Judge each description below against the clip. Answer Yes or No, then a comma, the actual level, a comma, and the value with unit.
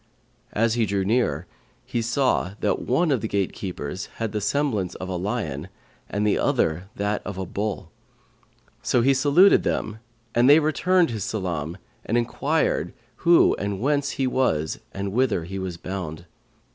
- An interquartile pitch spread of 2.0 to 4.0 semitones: No, average, 5.3 semitones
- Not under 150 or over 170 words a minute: Yes, average, 160 wpm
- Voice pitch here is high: No, low, 105 Hz